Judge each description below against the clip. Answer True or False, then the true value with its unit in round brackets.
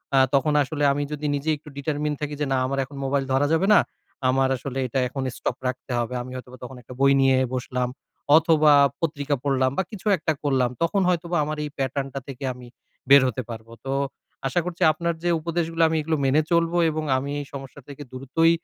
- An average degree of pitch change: True (3.1 semitones)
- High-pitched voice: False (140 Hz)